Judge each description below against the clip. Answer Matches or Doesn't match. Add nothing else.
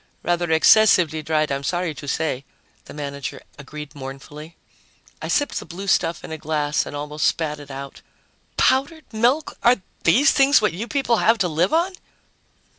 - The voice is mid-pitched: Matches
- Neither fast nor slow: Matches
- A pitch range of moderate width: Doesn't match